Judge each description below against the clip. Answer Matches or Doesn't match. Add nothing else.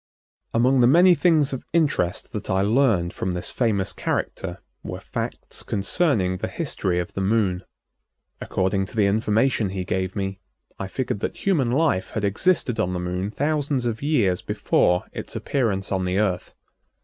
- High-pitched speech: Doesn't match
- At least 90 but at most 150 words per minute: Doesn't match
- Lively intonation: Matches